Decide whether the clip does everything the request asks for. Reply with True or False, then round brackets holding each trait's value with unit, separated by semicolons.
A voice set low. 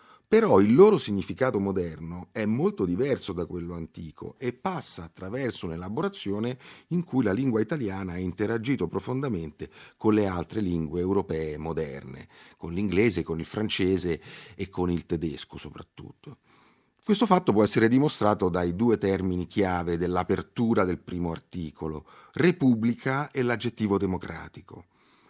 True (100 Hz)